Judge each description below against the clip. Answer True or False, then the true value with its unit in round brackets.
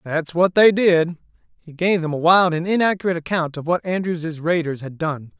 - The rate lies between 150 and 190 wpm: False (200 wpm)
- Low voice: False (170 Hz)